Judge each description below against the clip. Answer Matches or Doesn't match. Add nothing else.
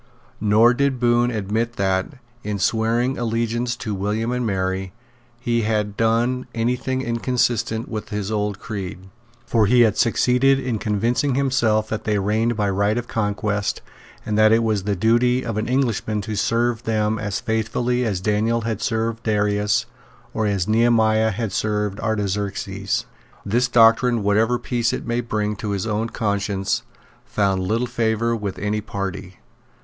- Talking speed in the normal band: Matches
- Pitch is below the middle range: Matches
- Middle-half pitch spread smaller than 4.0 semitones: Matches